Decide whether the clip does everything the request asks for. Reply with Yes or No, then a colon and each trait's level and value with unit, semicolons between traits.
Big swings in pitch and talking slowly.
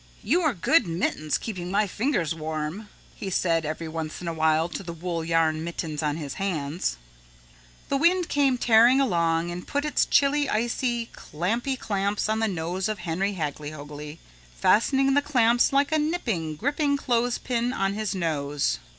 No: wide, 7.2 semitones; average, 165 wpm